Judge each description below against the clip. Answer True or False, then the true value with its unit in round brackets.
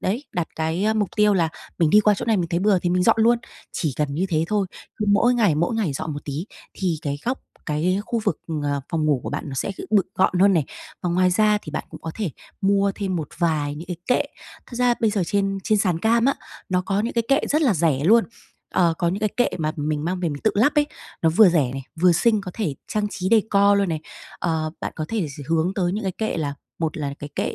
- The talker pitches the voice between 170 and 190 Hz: True (185 Hz)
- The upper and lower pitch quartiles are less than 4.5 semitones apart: False (4.9 semitones)